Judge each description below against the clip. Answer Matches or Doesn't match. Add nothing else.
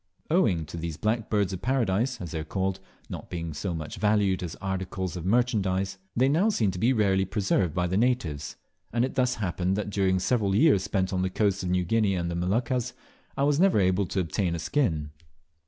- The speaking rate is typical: Doesn't match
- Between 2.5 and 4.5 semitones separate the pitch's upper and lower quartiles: Matches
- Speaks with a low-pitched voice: Matches